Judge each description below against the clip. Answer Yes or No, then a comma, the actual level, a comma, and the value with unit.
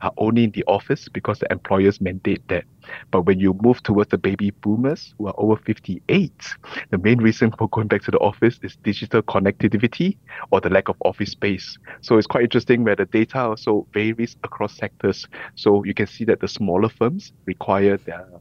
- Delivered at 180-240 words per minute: Yes, average, 200 wpm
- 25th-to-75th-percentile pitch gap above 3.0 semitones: No, narrow, 2.6 semitones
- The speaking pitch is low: Yes, low, 110 Hz